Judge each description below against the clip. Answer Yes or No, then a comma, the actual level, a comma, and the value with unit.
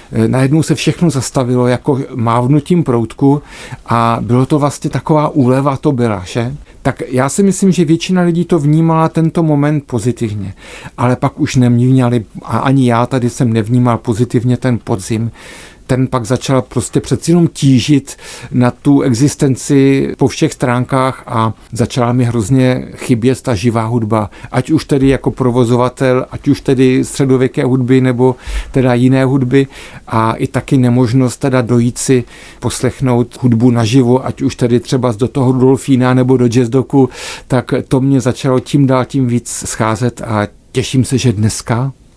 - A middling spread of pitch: No, narrow, 2.2 semitones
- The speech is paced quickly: No, average, 160 wpm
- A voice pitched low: Yes, low, 130 Hz